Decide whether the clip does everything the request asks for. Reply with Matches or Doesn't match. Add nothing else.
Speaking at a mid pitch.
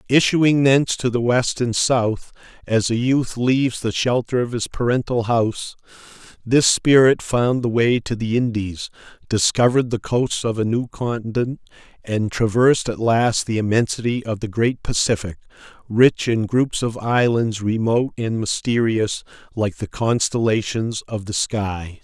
Doesn't match